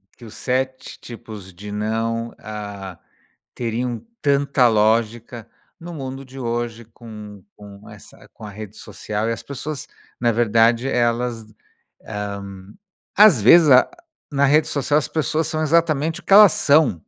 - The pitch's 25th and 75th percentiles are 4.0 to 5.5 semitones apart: Yes, average, 4.3 semitones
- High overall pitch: No, low, 120 Hz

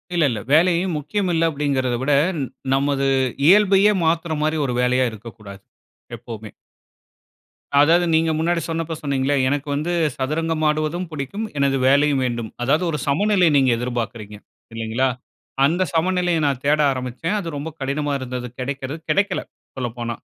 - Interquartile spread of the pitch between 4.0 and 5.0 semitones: Yes, average, 4.3 semitones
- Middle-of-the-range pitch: Yes, medium, 145 Hz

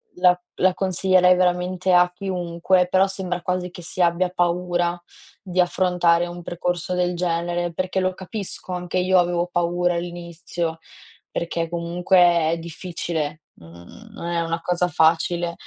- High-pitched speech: No, medium, 175 Hz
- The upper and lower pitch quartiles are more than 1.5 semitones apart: No, narrow, 1.1 semitones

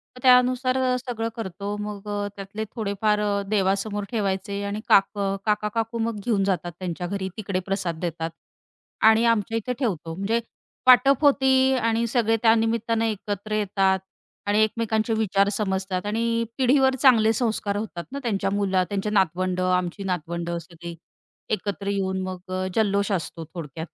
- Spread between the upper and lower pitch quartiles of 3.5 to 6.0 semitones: No, average, 3.0 semitones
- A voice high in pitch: Yes, high, 205 Hz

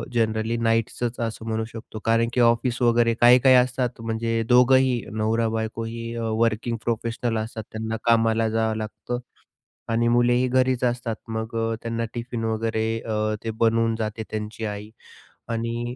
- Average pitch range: No, narrow, 1.2 semitones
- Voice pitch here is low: Yes, low, 115 Hz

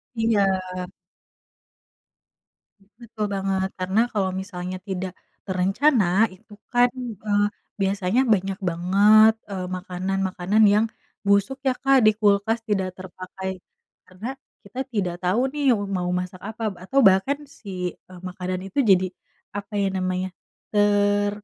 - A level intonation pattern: Yes, narrow, 2.3 semitones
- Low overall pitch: No, high, 195 Hz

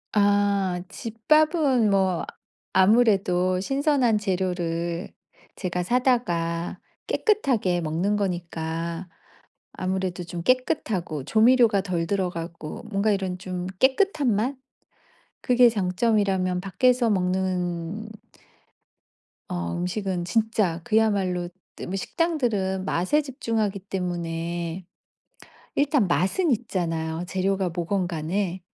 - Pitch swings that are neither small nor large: Yes, average, 4.1 semitones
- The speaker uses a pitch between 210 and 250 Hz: No, high, 190 Hz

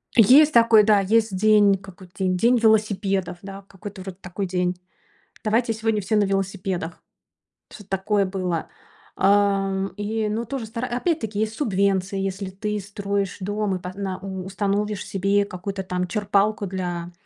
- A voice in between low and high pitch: No, high, 200 Hz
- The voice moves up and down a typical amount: No, narrow, 2.1 semitones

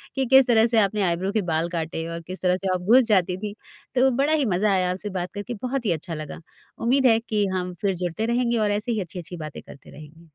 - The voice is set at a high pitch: Yes, high, 200 Hz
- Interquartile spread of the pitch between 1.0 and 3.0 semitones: No, average, 4.5 semitones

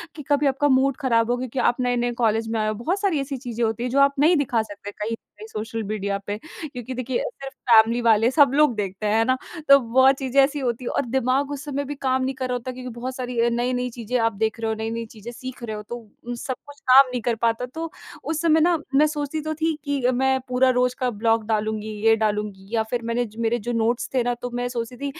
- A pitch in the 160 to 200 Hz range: No, high, 245 Hz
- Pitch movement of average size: Yes, average, 3.1 semitones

